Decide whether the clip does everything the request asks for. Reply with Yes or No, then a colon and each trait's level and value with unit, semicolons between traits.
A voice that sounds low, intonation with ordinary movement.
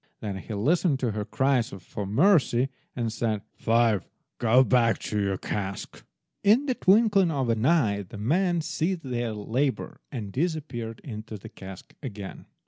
No: low, 120 Hz; wide, 6.6 semitones